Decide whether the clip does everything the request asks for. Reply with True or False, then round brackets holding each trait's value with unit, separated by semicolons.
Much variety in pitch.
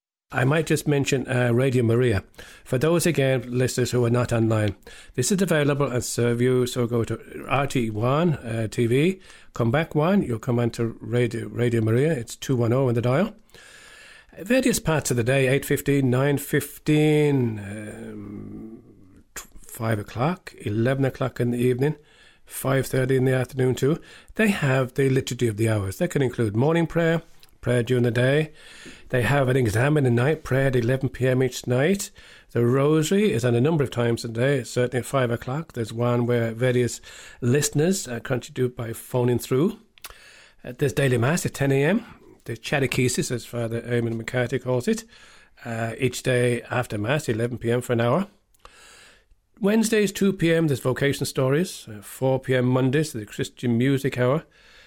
False (3.3 semitones)